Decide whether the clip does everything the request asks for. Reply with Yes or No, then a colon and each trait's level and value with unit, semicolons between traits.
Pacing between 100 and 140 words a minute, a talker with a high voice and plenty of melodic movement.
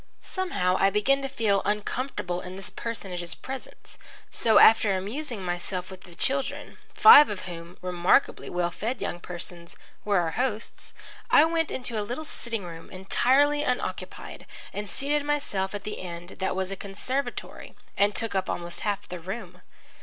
No: average, 160 wpm; high, 200 Hz; wide, 5.8 semitones